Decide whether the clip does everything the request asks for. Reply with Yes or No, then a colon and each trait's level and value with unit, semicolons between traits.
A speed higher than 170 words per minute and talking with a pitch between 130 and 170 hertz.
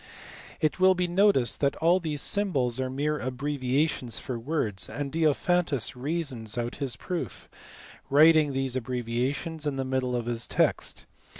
No: average, 155 wpm; medium, 140 Hz